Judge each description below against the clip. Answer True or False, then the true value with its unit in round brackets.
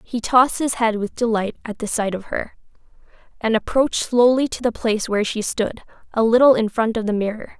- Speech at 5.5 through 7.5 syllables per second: True (5.8 syllables/s)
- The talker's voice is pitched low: False (225 Hz)